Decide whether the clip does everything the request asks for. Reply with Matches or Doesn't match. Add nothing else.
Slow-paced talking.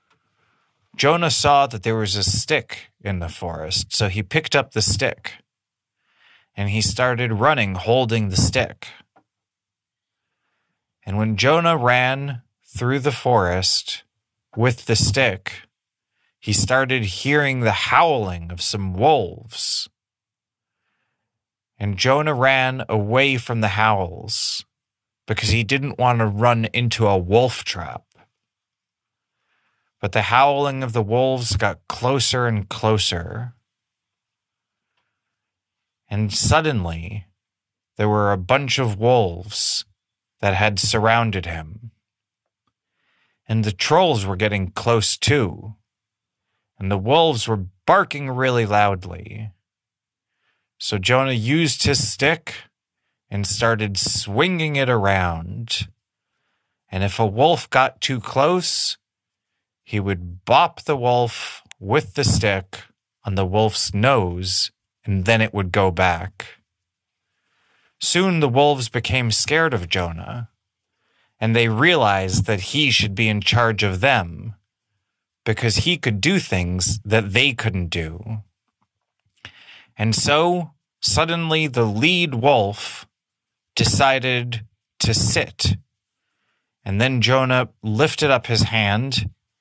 Matches